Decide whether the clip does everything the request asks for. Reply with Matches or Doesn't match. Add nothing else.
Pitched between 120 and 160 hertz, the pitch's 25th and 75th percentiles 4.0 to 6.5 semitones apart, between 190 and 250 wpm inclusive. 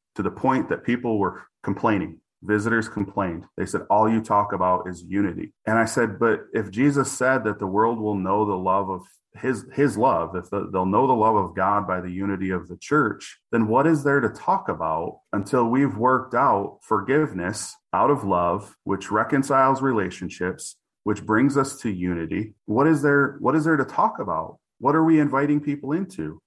Doesn't match